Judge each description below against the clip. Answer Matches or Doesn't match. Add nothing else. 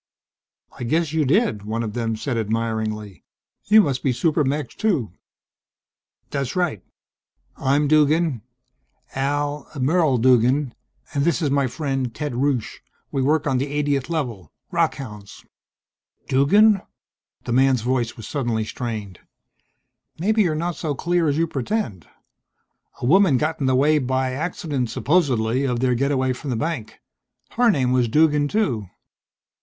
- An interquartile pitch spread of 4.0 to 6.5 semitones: Matches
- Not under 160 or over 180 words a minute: Doesn't match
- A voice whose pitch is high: Doesn't match